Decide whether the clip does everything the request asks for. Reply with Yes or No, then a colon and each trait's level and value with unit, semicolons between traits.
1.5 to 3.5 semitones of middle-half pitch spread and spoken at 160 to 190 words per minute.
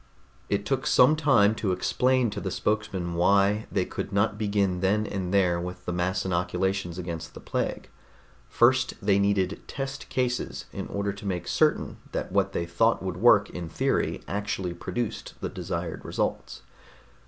Yes: average, 2.9 semitones; average, 165 wpm